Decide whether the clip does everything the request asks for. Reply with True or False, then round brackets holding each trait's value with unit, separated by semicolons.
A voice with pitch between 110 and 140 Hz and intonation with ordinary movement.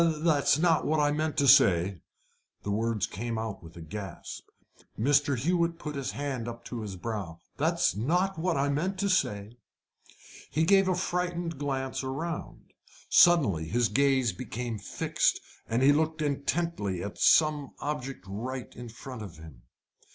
False (135 Hz; 6.5 semitones)